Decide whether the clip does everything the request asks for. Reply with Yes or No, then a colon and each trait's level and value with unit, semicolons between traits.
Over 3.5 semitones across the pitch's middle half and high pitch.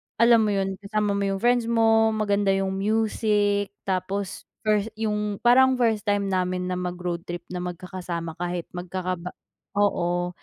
No: average, 3.0 semitones; high, 200 Hz